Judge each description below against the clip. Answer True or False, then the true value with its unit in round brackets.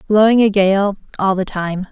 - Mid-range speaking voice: False (200 Hz)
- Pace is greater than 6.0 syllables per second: False (4.6 syllables/s)